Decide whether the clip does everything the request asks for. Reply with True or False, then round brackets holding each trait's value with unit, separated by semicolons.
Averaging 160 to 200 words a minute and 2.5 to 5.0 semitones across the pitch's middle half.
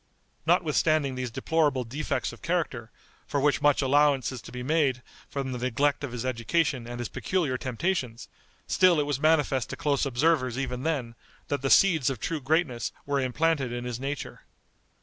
True (175 wpm; 3.5 semitones)